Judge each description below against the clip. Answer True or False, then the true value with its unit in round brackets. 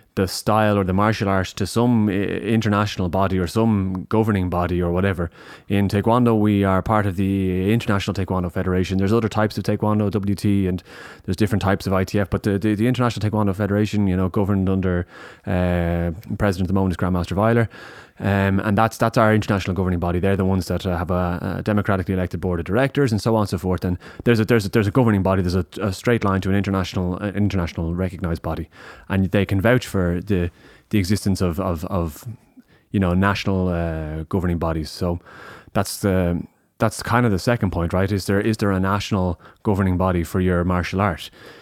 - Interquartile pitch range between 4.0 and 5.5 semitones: False (2.5 semitones)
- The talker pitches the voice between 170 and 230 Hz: False (95 Hz)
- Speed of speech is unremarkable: False (210 wpm)